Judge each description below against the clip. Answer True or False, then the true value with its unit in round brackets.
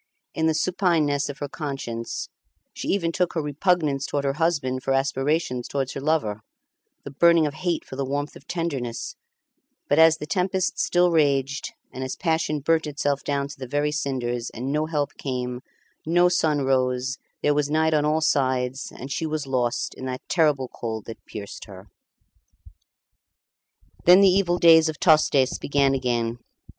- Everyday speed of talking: True (170 wpm)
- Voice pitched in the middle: True (145 Hz)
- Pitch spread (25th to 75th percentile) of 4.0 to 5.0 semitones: False (3.5 semitones)